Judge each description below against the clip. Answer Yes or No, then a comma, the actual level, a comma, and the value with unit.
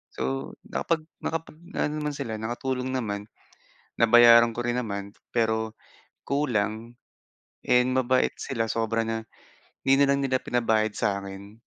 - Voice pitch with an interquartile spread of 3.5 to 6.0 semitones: No, average, 2.7 semitones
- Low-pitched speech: Yes, low, 120 Hz